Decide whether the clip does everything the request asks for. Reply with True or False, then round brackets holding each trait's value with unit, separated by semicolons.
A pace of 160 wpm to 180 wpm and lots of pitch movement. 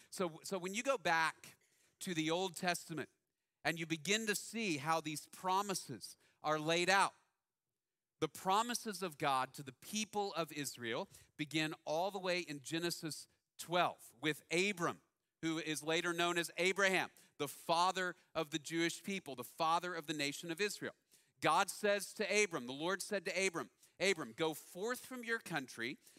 False (165 wpm; 3.6 semitones)